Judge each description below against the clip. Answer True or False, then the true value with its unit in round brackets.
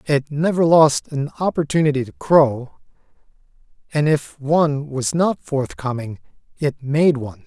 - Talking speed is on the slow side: True (130 wpm)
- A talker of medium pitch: True (145 Hz)